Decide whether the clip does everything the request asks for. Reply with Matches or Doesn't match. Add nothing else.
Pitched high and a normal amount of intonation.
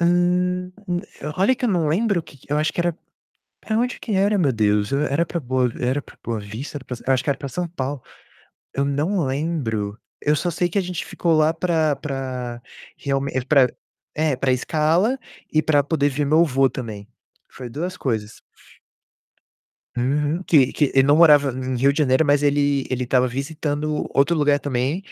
Doesn't match